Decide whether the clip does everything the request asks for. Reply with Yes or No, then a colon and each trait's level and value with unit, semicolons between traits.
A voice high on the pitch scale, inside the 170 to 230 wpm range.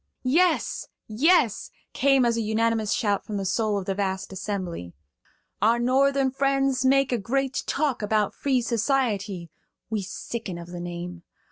No: high, 225 Hz; average, 150 wpm